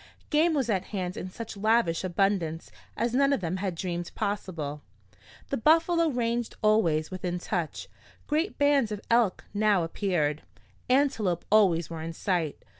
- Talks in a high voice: Yes, high, 200 Hz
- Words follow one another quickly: No, average, 150 wpm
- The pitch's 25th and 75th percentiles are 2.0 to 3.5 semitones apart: No, wide, 5.5 semitones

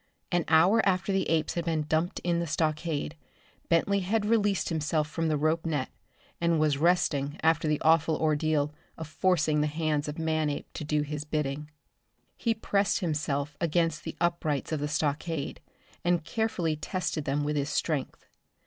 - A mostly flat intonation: Yes, narrow, 2.2 semitones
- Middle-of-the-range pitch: Yes, medium, 155 Hz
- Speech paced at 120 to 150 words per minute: No, average, 165 wpm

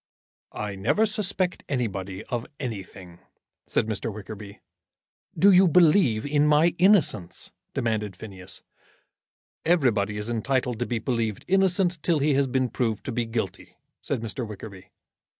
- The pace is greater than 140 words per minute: No, slow, 135 wpm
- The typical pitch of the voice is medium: No, low, 120 Hz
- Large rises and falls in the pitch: Yes, wide, 6.5 semitones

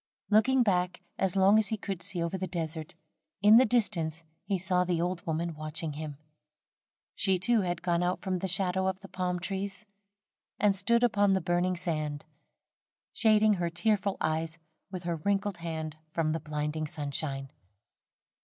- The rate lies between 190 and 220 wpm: No, average, 165 wpm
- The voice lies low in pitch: No, medium, 180 Hz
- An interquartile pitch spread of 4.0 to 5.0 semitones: No, average, 3.4 semitones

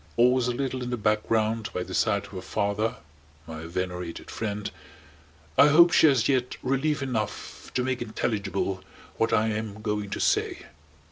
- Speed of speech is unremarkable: Yes, average, 165 wpm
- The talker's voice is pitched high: No, low, 110 Hz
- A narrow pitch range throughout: No, average, 3.6 semitones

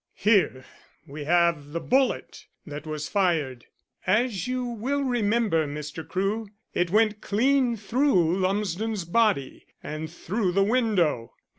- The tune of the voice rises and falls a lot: Yes, wide, 6.2 semitones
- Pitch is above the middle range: Yes, high, 195 Hz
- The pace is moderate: No, slow, 125 wpm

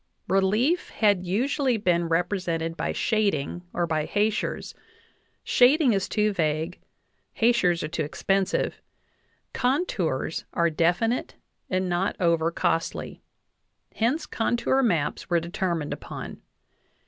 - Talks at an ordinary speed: No, slow, 115 wpm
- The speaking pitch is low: No, medium, 185 Hz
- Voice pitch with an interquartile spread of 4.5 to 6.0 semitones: Yes, average, 5.0 semitones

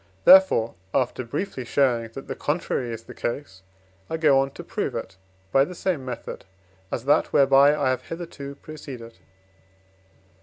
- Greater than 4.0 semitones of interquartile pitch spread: No, average, 3.7 semitones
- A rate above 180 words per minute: No, average, 155 wpm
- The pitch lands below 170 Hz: Yes, low, 135 Hz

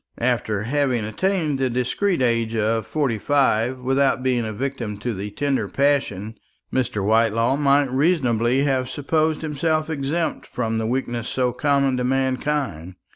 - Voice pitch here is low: Yes, low, 130 Hz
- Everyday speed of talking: Yes, average, 145 wpm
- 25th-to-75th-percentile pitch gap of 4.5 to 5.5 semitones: No, average, 3.7 semitones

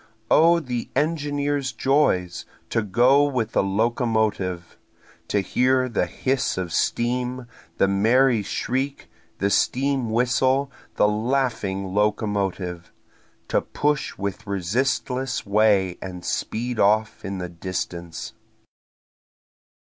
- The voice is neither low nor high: No, low, 115 Hz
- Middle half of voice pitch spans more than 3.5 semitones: Yes, average, 5.1 semitones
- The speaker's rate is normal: No, slow, 105 wpm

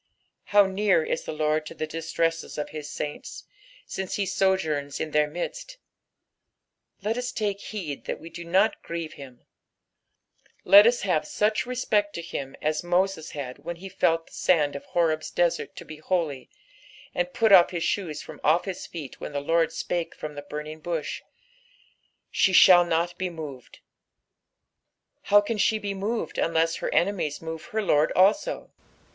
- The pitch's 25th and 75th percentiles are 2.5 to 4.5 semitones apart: Yes, average, 4.1 semitones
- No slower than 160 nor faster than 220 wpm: Yes, average, 170 wpm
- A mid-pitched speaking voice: Yes, medium, 170 Hz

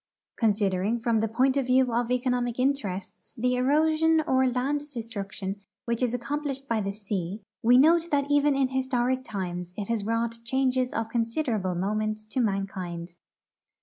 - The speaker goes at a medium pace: Yes, average, 155 wpm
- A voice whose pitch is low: No, high, 235 Hz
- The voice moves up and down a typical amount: Yes, average, 4.1 semitones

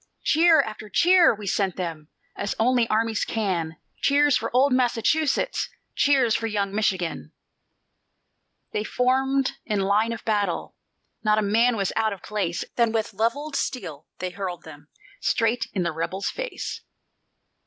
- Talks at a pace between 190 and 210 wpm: No, average, 145 wpm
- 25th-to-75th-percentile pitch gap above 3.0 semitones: Yes, average, 4.5 semitones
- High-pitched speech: Yes, high, 220 Hz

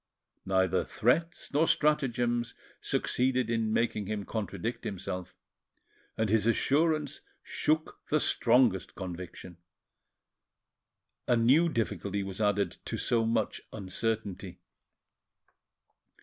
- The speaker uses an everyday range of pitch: Yes, average, 4.2 semitones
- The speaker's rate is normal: No, slow, 95 wpm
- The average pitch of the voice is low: Yes, low, 115 Hz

